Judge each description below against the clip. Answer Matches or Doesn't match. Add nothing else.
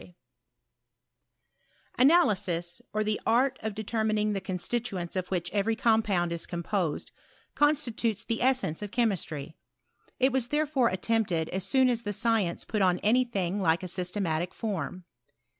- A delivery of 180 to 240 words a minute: Doesn't match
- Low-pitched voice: Doesn't match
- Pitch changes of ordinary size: Matches